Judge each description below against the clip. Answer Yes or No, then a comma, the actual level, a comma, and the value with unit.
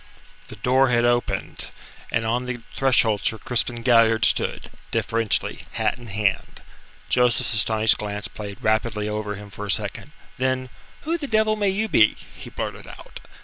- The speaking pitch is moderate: No, low, 115 Hz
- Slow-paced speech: No, average, 160 wpm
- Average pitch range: Yes, average, 3.1 semitones